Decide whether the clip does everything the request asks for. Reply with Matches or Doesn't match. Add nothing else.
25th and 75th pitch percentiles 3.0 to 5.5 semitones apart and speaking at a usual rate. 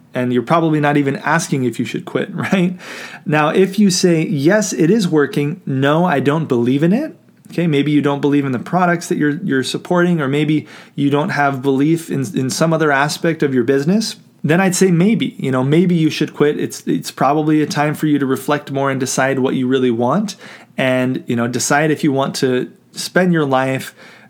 Doesn't match